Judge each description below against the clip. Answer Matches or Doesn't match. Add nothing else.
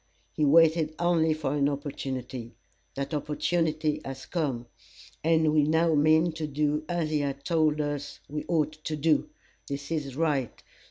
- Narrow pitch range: Matches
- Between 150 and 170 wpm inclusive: Matches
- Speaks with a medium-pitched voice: Matches